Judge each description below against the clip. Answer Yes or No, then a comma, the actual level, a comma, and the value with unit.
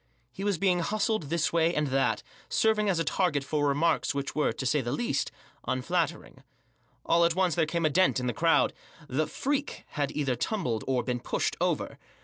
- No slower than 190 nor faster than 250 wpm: Yes, average, 195 wpm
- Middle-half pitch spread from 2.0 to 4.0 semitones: No, average, 4.8 semitones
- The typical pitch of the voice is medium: Yes, medium, 160 Hz